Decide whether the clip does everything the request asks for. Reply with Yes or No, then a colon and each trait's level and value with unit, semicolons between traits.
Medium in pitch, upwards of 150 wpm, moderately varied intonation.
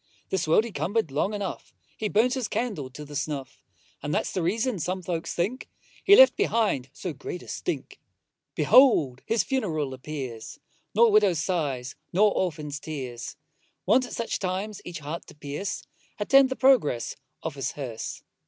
No: medium, 175 Hz; average, 165 wpm; wide, 7.1 semitones